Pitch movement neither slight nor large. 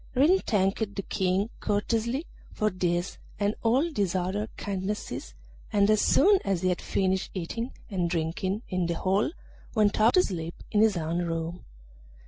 Yes: average, 3.3 semitones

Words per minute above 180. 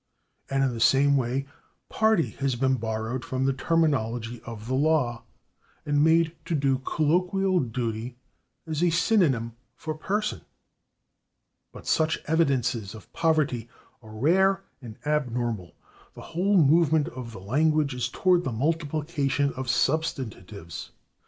No: slow, 135 wpm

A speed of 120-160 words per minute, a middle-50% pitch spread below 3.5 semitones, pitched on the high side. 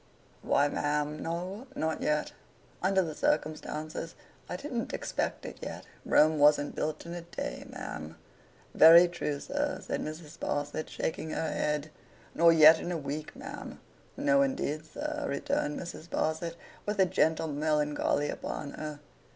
No: average, 145 wpm; narrow, 2.6 semitones; medium, 155 Hz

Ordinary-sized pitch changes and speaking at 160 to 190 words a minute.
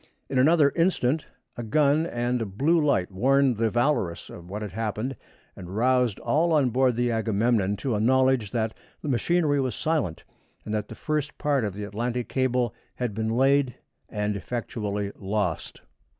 Yes: average, 4.6 semitones; average, 170 wpm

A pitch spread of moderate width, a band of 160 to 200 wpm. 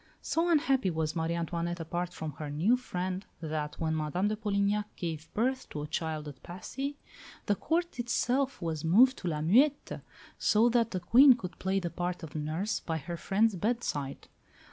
No: wide, 6.5 semitones; average, 180 wpm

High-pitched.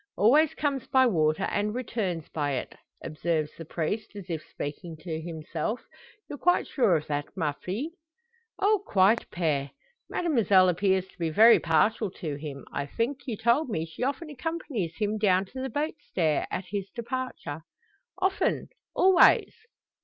Yes: high, 195 Hz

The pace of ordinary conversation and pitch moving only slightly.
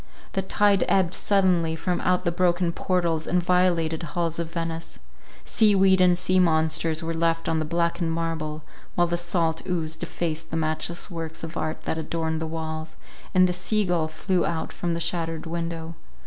Yes: average, 180 wpm; narrow, 1.8 semitones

